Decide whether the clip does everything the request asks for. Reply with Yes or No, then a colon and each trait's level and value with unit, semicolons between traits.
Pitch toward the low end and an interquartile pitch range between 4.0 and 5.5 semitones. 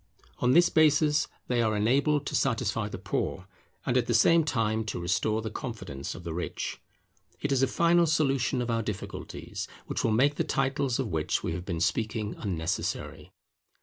Yes: low, 115 Hz; average, 4.9 semitones